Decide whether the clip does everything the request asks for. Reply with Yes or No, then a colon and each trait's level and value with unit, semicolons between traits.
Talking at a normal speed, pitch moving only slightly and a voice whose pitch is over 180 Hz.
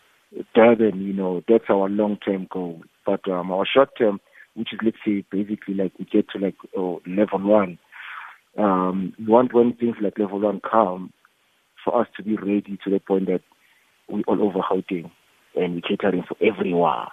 No: average, 185 wpm; narrow, 2.1 semitones; low, 100 Hz